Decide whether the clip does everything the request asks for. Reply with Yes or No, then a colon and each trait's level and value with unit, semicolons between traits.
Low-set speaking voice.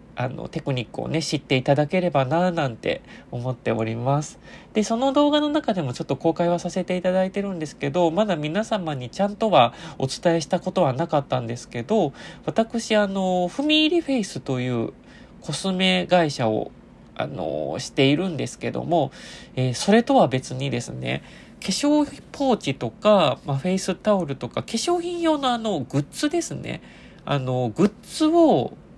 No: medium, 175 Hz